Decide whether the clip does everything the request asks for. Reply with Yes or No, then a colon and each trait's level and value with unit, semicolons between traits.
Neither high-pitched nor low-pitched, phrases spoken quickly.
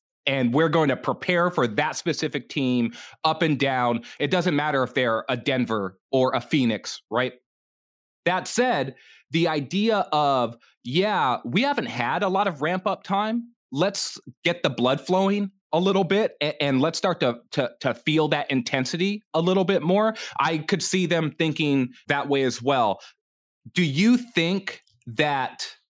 No: medium, 160 Hz; average, 165 wpm